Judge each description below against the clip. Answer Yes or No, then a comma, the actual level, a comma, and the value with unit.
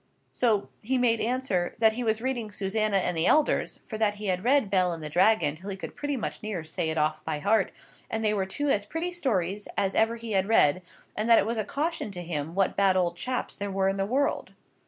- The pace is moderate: No, fast, 240 wpm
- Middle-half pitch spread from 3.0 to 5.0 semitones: Yes, average, 3.8 semitones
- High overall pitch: Yes, high, 210 Hz